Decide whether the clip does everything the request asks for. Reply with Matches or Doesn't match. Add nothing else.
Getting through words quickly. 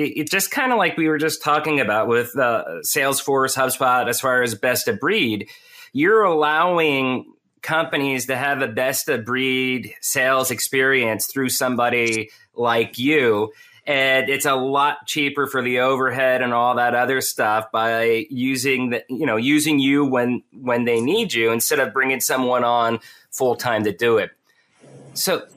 Doesn't match